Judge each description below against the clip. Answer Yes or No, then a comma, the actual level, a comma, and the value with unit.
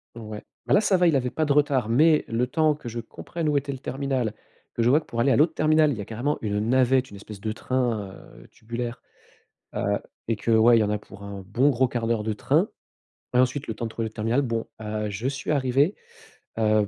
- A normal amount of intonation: Yes, average, 4.4 semitones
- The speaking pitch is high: No, low, 120 Hz